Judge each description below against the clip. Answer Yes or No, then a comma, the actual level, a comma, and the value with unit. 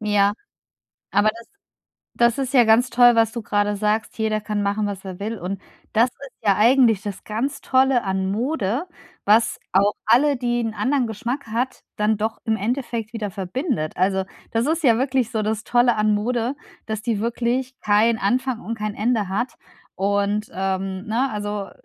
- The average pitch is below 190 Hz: No, high, 220 Hz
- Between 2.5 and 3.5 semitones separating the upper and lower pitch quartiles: Yes, average, 2.9 semitones